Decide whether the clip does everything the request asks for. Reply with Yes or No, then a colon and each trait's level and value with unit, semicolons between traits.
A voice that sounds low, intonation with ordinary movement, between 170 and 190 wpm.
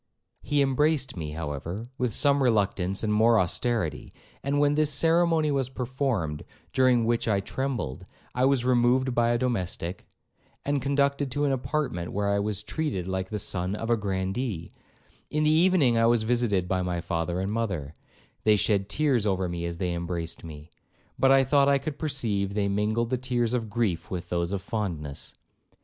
No: low, 115 Hz; wide, 6.2 semitones; average, 180 wpm